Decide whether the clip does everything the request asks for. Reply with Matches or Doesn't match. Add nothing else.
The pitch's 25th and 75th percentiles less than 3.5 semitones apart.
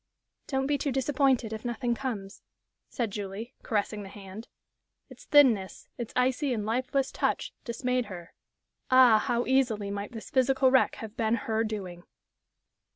Doesn't match